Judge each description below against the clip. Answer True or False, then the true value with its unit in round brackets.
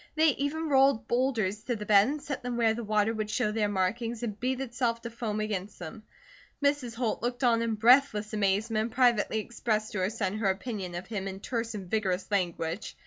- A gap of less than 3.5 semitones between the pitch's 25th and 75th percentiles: True (2.9 semitones)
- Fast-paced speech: True (210 wpm)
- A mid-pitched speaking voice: False (220 Hz)